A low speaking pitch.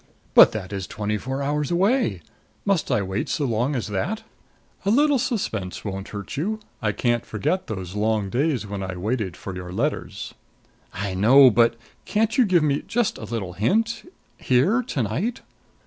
Yes: low, 120 Hz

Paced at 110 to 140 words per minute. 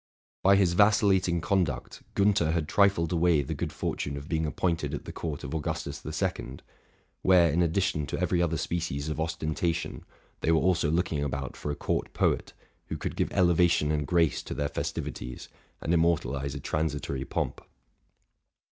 No: average, 175 wpm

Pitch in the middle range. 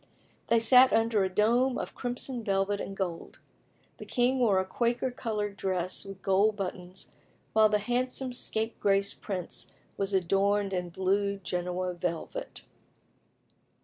No: high, 200 Hz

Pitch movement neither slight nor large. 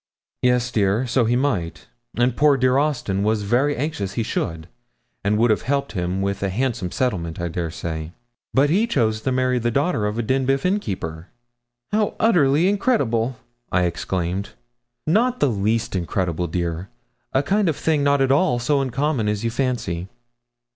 No: wide, 6.3 semitones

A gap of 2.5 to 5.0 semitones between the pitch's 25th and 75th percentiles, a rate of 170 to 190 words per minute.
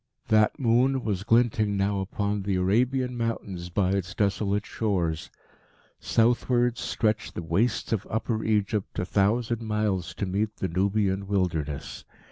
No: average, 3.0 semitones; slow, 135 wpm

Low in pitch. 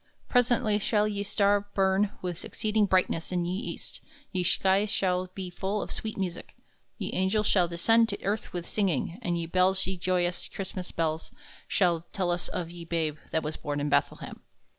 No: medium, 185 Hz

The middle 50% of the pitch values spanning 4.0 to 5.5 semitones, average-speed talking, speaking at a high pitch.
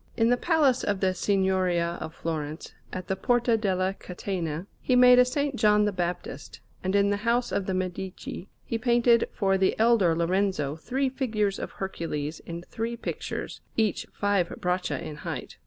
Yes: average, 4.6 semitones; average, 170 wpm; high, 195 Hz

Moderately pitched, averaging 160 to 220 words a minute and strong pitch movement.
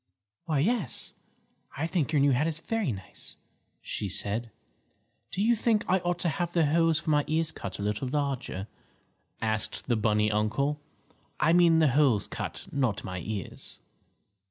Yes: medium, 145 Hz; average, 165 wpm; wide, 7.2 semitones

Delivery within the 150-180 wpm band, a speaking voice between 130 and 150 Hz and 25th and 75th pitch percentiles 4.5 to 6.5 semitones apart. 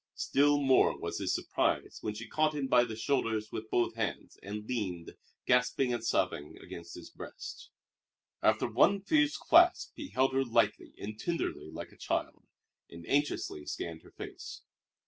No: average, 165 wpm; low, 120 Hz; average, 5.1 semitones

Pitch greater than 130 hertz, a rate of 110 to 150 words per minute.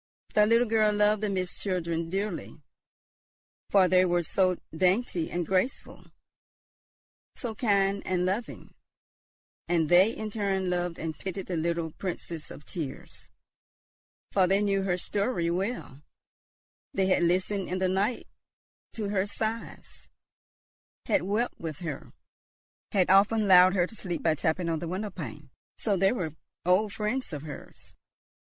Yes: medium, 185 Hz; average, 145 wpm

